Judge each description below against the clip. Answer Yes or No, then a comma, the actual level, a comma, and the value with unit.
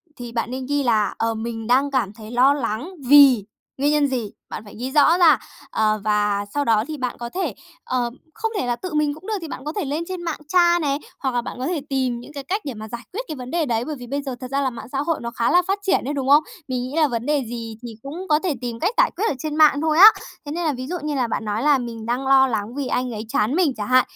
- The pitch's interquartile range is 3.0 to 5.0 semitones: Yes, average, 4.3 semitones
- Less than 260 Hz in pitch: No, very high, 265 Hz